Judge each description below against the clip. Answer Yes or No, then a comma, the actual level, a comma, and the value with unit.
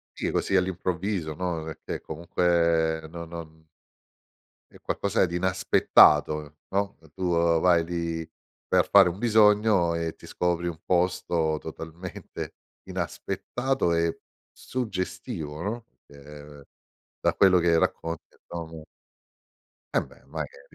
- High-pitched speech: No, very low, 85 Hz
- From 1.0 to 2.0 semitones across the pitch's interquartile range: No, narrow, 2.5 semitones